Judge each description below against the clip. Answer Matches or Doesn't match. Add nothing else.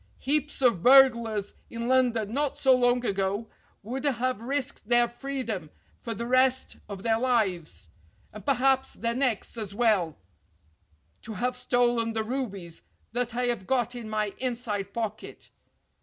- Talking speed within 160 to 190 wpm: Doesn't match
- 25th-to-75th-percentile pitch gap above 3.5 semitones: Doesn't match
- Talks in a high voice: Matches